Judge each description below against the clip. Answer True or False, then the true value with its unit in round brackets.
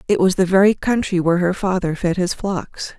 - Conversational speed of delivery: False (220 wpm)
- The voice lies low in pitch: False (185 Hz)